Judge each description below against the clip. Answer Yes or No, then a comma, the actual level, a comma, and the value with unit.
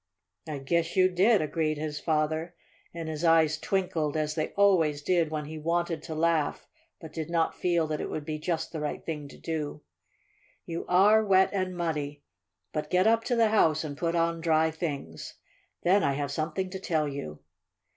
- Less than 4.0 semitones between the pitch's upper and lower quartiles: Yes, narrow, 2.4 semitones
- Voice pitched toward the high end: No, medium, 160 Hz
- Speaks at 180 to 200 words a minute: Yes, average, 190 wpm